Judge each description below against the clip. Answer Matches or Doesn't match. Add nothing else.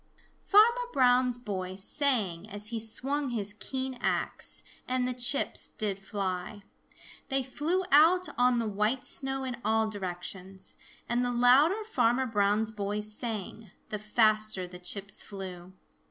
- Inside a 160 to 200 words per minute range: Doesn't match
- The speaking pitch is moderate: Doesn't match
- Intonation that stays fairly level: Doesn't match